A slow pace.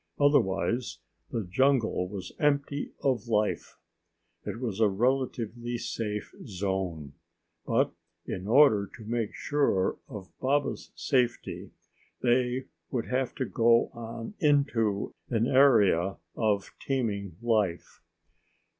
Yes: slow, 110 wpm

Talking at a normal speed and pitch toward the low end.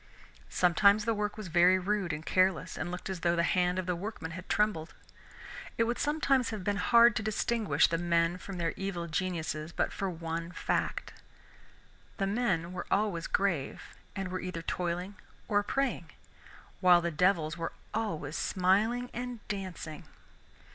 No: average, 160 wpm; medium, 185 Hz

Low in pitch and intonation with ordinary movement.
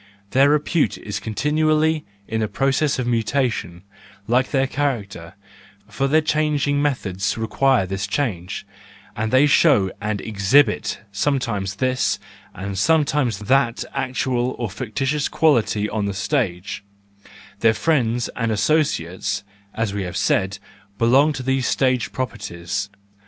No: low, 120 Hz; wide, 5.7 semitones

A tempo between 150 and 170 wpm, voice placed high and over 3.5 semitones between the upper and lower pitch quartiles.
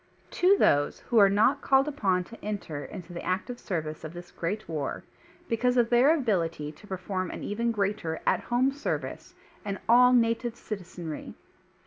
Yes: average, 165 wpm; high, 205 Hz; wide, 5.6 semitones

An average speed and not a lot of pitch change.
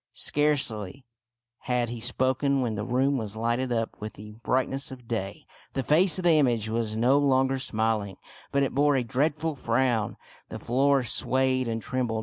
No: average, 170 wpm; average, 3.3 semitones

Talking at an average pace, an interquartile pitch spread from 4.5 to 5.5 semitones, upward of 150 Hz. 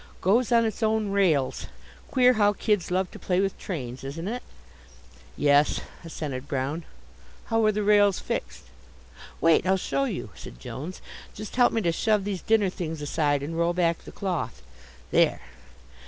Yes: average, 165 wpm; average, 5.2 semitones; medium, 185 Hz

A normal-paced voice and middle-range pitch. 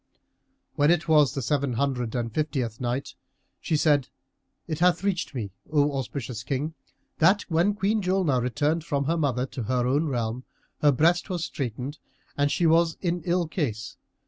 Yes: average, 170 wpm; medium, 145 Hz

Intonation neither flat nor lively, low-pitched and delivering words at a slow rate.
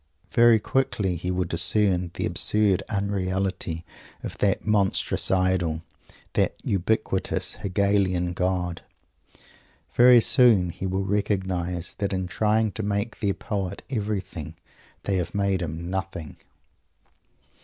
No: narrow, 2.3 semitones; very low, 95 Hz; slow, 115 wpm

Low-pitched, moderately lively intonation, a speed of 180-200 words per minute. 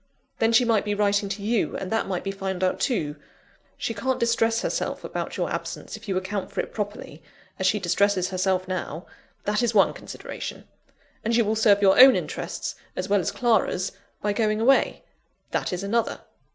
No: high, 205 Hz; average, 3.0 semitones; average, 190 wpm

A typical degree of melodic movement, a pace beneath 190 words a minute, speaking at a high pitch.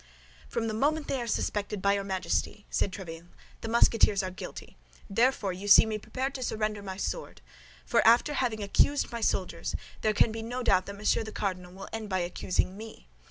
No: average, 3.2 semitones; average, 195 wpm; high, 215 Hz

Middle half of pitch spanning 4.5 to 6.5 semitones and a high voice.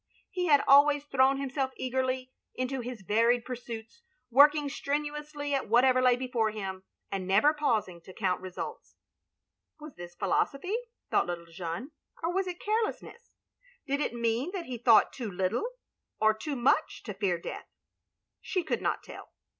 Yes: average, 5.2 semitones; very high, 255 Hz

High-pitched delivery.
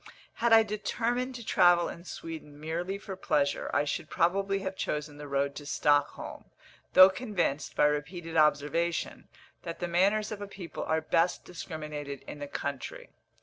No: medium, 170 Hz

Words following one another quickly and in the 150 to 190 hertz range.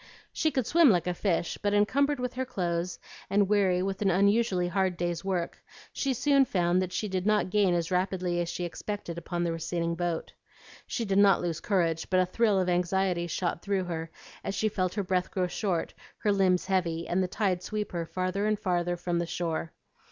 Yes: fast, 210 wpm; medium, 185 Hz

